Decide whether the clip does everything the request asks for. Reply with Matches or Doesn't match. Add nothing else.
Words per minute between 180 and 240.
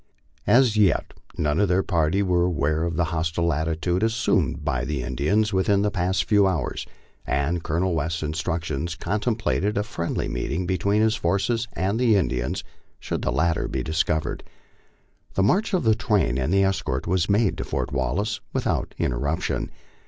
Doesn't match